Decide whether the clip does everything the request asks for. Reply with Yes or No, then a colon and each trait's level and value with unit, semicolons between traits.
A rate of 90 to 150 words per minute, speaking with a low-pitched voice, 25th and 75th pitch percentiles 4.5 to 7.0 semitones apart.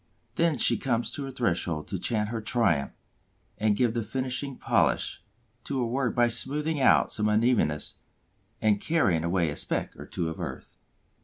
No: average, 170 wpm; low, 115 Hz; wide, 5.4 semitones